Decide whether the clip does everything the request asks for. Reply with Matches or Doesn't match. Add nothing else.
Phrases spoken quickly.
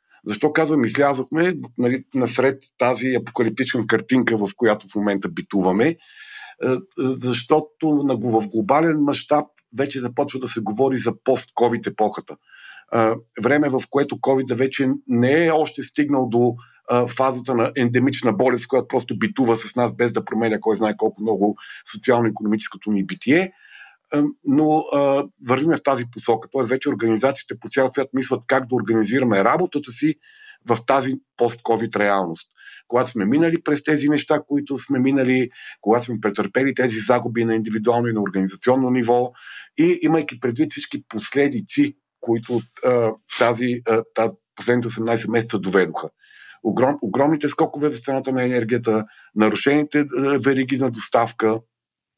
Doesn't match